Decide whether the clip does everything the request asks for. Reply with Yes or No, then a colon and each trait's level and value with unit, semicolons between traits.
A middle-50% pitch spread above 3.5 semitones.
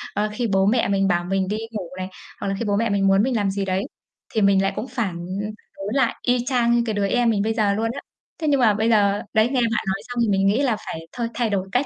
No: average, 3.2 semitones